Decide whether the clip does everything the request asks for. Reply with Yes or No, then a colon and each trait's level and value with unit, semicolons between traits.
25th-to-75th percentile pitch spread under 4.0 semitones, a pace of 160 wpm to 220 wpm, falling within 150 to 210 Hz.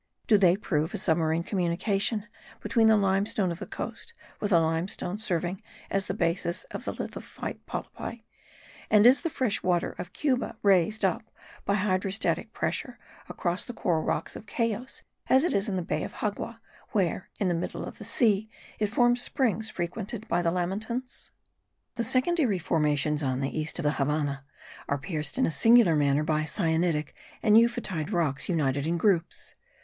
No: average, 5.0 semitones; average, 170 wpm; medium, 185 Hz